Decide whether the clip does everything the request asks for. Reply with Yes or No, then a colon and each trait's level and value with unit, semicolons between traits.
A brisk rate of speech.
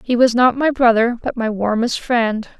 Yes: fast, 210 wpm